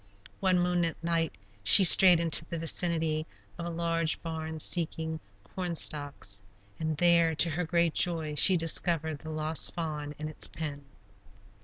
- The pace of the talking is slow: No, average, 150 wpm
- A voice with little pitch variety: Yes, narrow, 1.6 semitones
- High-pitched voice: No, medium, 165 Hz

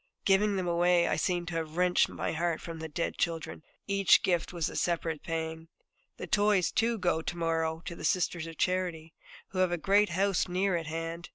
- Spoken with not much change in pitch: Yes, narrow, 2.2 semitones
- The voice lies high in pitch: No, medium, 175 Hz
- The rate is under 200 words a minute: No, fast, 205 wpm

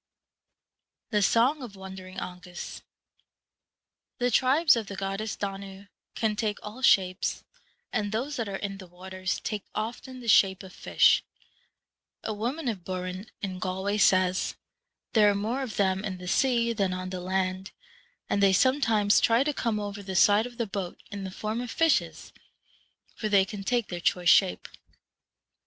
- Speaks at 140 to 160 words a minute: No, average, 170 wpm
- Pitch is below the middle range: No, high, 200 Hz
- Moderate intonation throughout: Yes, average, 3.4 semitones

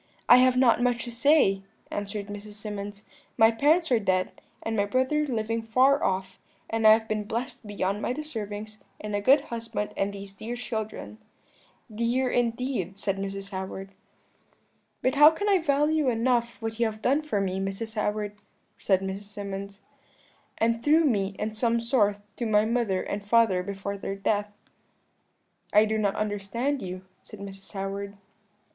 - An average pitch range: Yes, average, 3.3 semitones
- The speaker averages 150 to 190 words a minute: Yes, average, 165 wpm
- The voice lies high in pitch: Yes, high, 215 Hz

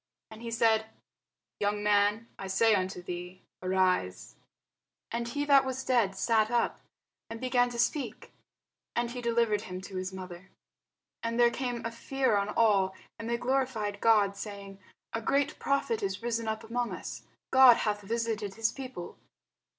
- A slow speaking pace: No, average, 160 wpm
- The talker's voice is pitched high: Yes, high, 225 Hz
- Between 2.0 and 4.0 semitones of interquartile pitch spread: Yes, average, 3.2 semitones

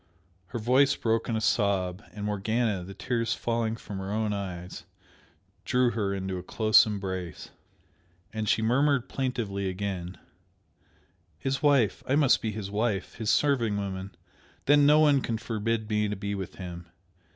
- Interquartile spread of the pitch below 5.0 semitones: Yes, average, 3.4 semitones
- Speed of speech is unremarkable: Yes, average, 160 wpm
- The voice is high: No, low, 110 Hz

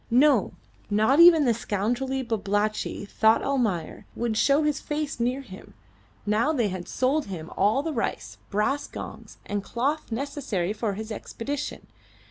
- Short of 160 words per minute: Yes, average, 145 wpm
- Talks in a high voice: Yes, high, 235 Hz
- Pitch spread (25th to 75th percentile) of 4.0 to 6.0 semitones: Yes, average, 5.2 semitones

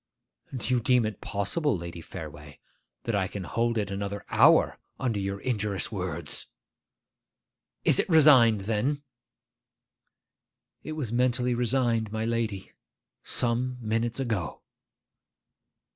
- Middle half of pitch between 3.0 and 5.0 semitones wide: Yes, average, 3.9 semitones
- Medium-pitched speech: No, low, 115 Hz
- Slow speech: Yes, slow, 115 wpm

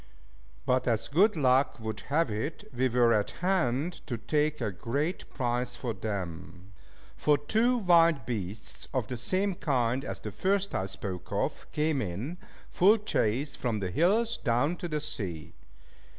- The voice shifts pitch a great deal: Yes, wide, 7.0 semitones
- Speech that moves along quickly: No, average, 160 wpm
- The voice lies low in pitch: Yes, low, 130 Hz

